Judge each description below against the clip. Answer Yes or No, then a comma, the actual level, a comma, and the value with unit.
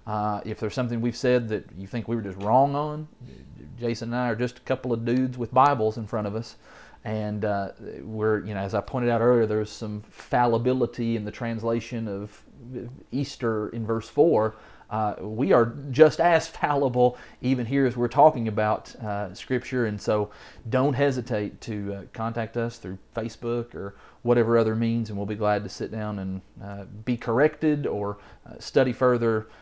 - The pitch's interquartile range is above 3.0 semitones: No, average, 2.7 semitones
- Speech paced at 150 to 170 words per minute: No, average, 190 wpm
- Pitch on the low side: Yes, low, 115 Hz